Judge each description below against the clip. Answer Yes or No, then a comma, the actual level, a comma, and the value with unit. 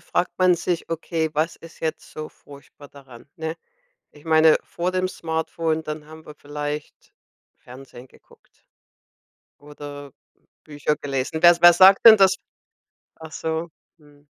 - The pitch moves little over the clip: Yes, narrow, 2.3 semitones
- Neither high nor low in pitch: Yes, medium, 155 Hz